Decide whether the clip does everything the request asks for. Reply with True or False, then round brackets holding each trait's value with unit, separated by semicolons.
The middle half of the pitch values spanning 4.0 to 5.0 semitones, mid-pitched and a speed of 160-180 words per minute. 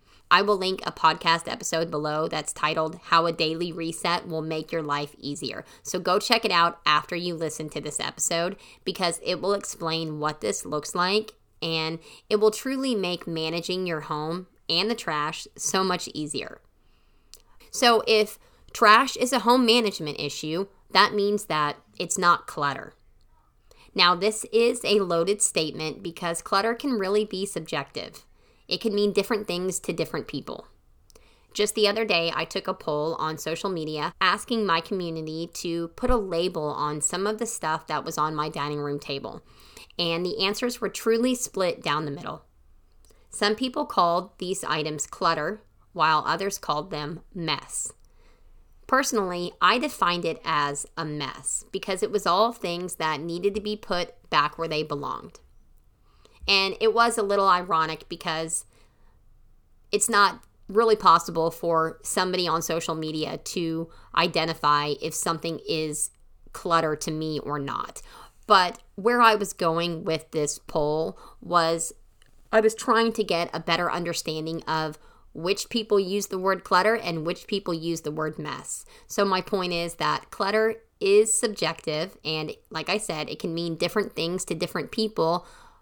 True (4.6 semitones; 170 Hz; 165 wpm)